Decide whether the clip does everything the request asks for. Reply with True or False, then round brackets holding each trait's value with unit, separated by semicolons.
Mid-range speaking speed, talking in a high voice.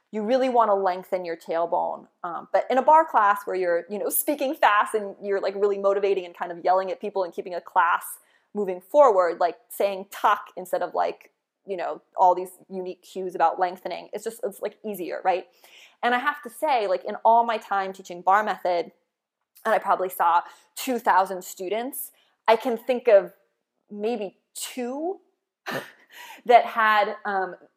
True (185 wpm; 200 Hz)